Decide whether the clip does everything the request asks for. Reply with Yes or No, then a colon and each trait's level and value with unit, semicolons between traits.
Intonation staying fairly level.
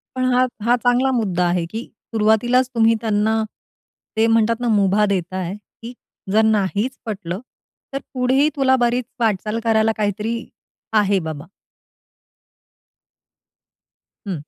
No: average, 3.1 semitones